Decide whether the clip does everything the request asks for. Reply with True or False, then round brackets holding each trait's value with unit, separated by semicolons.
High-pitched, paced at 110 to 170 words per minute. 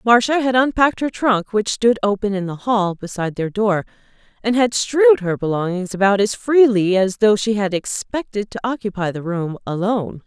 False (210 Hz; 185 wpm)